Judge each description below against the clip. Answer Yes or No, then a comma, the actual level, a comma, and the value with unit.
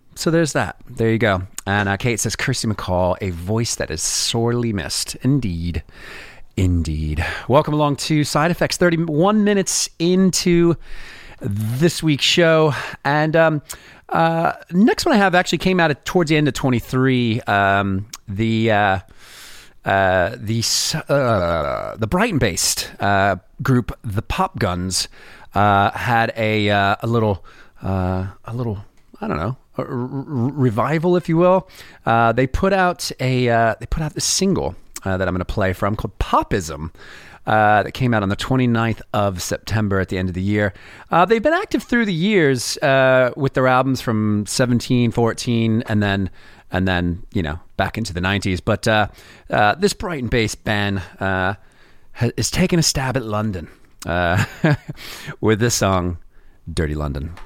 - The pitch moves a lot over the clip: Yes, wide, 6.9 semitones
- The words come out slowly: No, average, 165 wpm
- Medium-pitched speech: No, low, 115 Hz